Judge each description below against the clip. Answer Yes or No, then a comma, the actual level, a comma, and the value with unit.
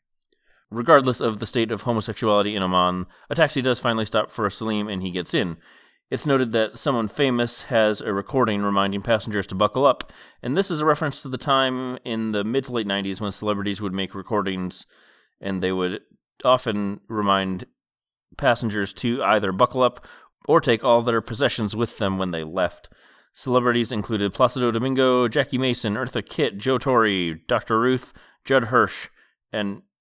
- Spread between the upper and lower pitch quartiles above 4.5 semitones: No, average, 3.8 semitones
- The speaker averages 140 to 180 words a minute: Yes, average, 175 wpm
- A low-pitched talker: Yes, low, 110 Hz